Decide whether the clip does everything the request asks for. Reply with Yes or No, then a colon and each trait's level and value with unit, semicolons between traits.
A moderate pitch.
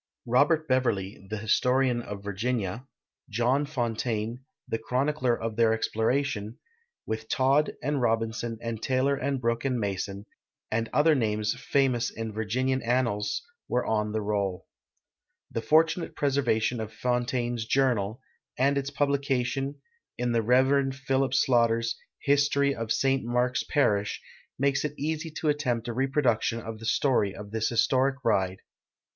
No: low, 120 Hz